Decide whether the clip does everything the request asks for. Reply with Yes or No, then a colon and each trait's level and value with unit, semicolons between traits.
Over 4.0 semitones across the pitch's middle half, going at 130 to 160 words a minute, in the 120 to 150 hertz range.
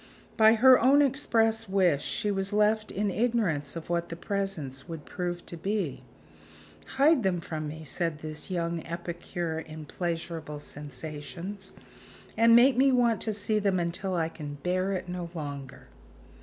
No: average, 5.0 semitones; average, 155 wpm; medium, 180 Hz